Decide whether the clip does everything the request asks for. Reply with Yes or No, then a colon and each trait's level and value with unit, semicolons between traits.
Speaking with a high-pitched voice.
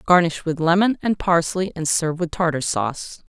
No: medium, 170 Hz